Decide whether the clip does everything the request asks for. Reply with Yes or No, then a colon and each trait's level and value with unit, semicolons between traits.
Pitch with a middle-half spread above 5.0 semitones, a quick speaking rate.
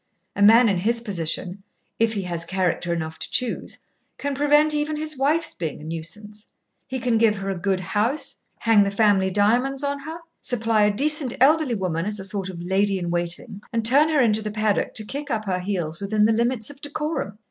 Yes: wide, 5.5 semitones; fast, 210 wpm